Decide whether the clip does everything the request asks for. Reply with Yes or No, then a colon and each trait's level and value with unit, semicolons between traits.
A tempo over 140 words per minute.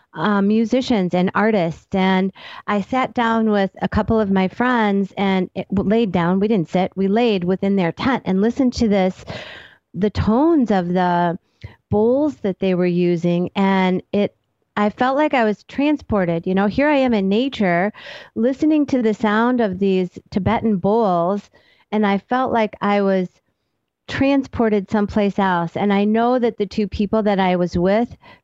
Yes: average, 175 wpm